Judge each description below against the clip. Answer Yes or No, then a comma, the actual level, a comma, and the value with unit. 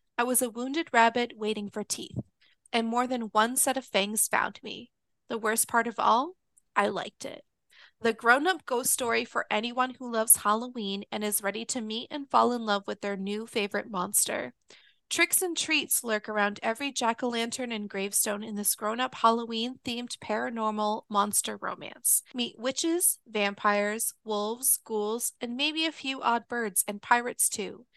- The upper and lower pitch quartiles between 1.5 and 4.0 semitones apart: Yes, average, 2.8 semitones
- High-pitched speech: Yes, high, 230 Hz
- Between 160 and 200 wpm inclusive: Yes, average, 180 wpm